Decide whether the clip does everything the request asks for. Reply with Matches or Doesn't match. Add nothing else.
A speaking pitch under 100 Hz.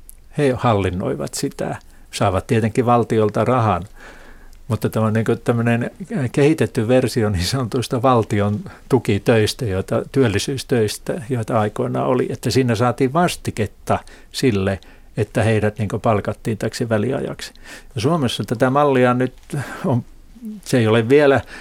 Doesn't match